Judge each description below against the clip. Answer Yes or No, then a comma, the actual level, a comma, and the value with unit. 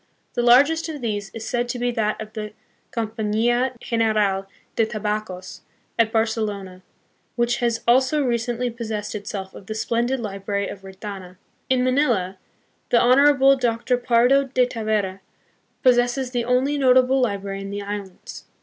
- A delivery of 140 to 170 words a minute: Yes, average, 145 wpm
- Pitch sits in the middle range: No, high, 230 Hz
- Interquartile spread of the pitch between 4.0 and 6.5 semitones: No, average, 3.3 semitones